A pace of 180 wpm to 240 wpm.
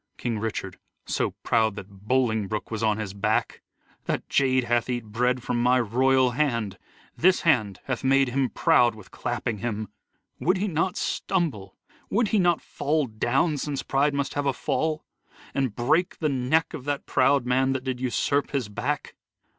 No: average, 170 wpm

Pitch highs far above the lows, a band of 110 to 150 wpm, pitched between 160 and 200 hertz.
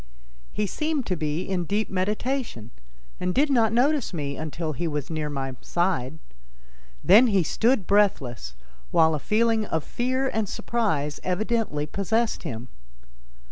Yes: wide, 7.1 semitones; average, 140 wpm; medium, 185 Hz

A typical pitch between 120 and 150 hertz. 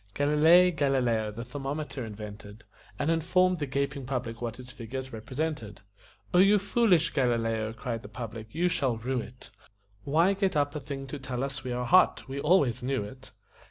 Yes: low, 135 Hz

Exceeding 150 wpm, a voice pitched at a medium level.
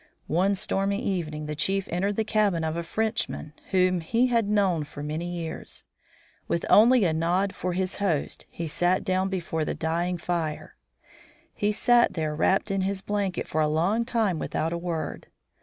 Yes: average, 175 wpm; medium, 180 Hz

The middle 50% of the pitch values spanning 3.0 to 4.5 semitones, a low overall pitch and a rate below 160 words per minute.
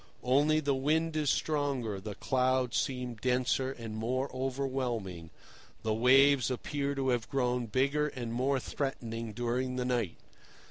No: narrow, 2.6 semitones; low, 130 Hz; average, 140 wpm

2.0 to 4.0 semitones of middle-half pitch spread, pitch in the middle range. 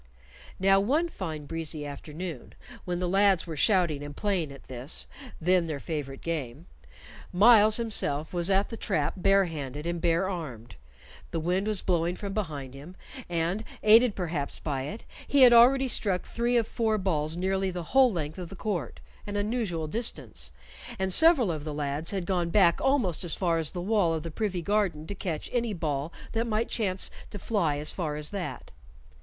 No: average, 4.8 semitones; medium, 180 Hz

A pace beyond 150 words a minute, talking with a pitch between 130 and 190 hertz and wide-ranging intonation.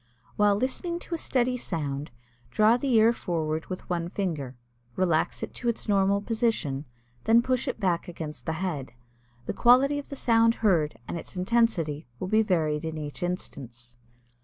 Yes: average, 170 wpm; medium, 185 Hz; wide, 6.6 semitones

